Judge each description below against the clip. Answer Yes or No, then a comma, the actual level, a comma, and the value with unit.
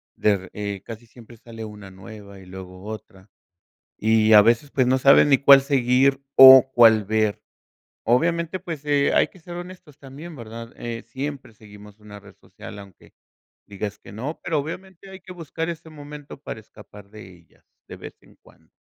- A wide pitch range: Yes, wide, 5.7 semitones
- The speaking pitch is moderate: No, low, 115 Hz